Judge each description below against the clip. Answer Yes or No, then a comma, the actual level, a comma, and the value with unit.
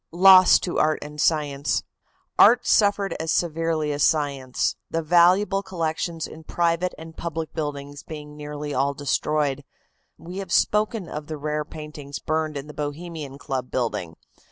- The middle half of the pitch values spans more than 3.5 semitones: No, narrow, 2.5 semitones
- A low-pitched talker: No, medium, 155 Hz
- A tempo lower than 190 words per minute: Yes, average, 150 wpm